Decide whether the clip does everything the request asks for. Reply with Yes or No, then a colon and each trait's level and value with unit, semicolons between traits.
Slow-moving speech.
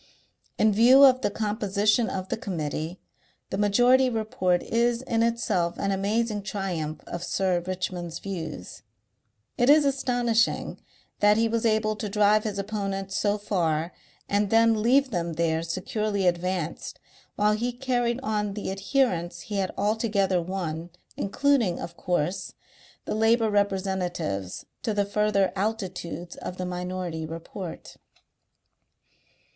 Yes: slow, 130 wpm